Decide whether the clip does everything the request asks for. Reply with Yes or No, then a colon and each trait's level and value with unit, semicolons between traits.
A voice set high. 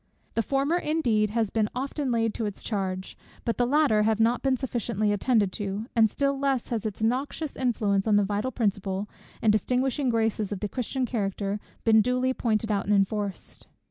Yes: high, 225 Hz